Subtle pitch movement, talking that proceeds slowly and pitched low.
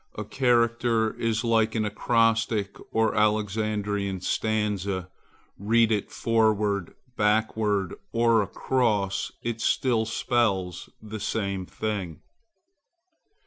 Yes: narrow, 2.1 semitones; slow, 90 wpm; low, 110 Hz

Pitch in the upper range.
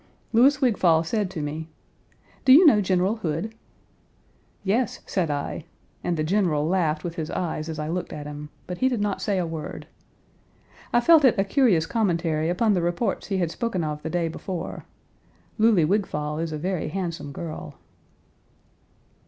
No: medium, 175 Hz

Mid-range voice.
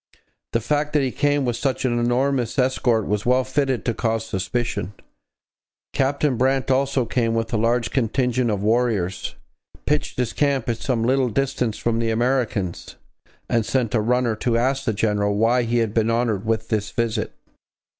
No: low, 120 Hz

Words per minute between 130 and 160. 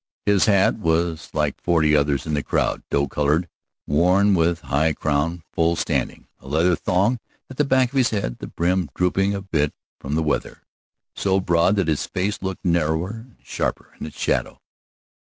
No: average, 185 wpm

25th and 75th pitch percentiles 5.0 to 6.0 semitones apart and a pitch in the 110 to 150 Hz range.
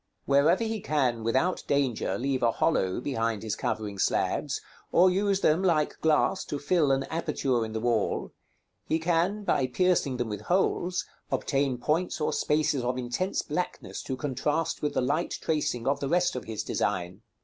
Yes: wide, 5.4 semitones; medium, 140 Hz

